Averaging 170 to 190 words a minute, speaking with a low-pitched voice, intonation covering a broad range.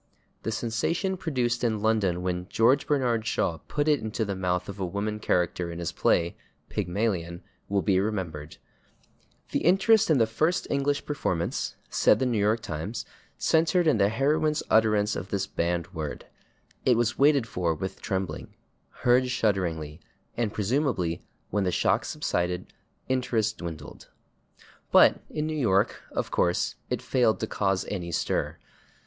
No: average, 155 wpm; low, 105 Hz; wide, 5.9 semitones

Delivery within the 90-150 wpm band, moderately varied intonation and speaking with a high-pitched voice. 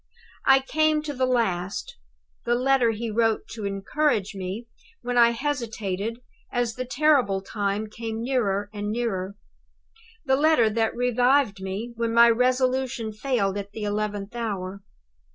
Yes: average, 140 wpm; average, 3.7 semitones; high, 230 Hz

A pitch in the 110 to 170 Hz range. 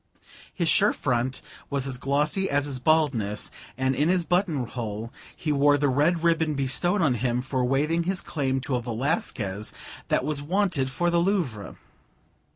Yes: medium, 140 Hz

